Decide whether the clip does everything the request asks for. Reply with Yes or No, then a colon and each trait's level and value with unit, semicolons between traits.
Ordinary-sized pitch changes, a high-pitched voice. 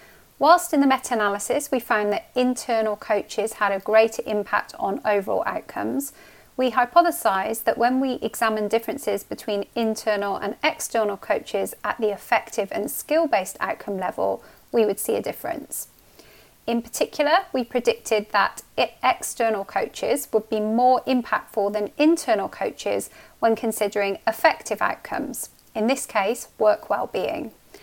Yes: average, 3.7 semitones; high, 225 Hz